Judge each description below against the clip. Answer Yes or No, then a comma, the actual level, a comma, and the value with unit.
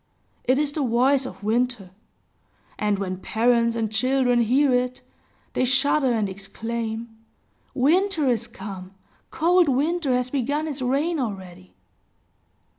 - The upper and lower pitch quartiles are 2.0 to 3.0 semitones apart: No, average, 4.0 semitones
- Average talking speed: No, slow, 125 wpm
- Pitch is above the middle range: Yes, very high, 250 Hz